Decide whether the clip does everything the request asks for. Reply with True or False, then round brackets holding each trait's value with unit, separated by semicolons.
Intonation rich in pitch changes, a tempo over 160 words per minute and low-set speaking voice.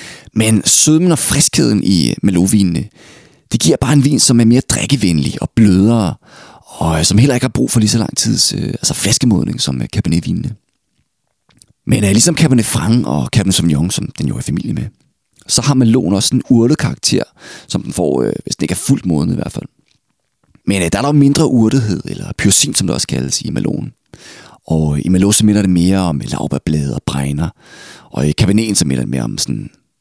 True (6.2 semitones; 200 wpm; 110 Hz)